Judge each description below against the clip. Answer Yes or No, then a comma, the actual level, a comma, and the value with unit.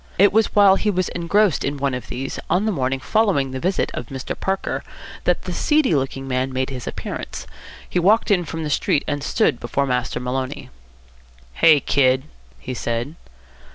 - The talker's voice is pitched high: No, medium, 140 Hz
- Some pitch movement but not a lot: No, wide, 6.4 semitones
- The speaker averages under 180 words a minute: No, average, 185 wpm